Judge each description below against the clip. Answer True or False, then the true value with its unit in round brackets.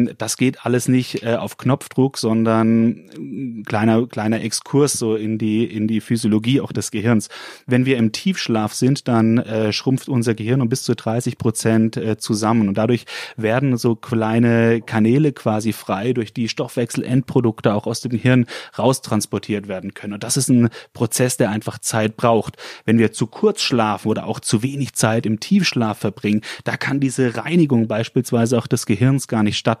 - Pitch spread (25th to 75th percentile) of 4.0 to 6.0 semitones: False (2.6 semitones)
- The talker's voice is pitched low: True (115 Hz)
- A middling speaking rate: True (170 wpm)